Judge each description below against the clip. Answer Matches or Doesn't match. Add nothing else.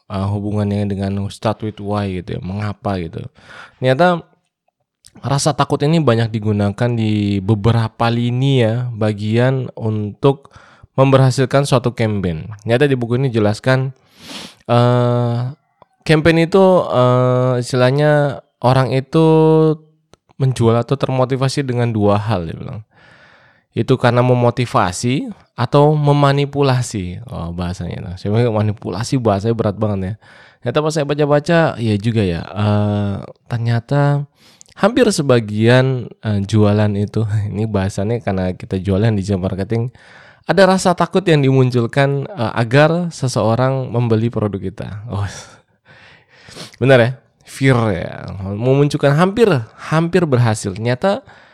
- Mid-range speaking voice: Doesn't match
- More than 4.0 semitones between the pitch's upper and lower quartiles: Matches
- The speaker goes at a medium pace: Matches